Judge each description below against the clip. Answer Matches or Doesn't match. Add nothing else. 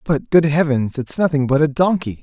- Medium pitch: Matches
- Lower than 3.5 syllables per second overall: Doesn't match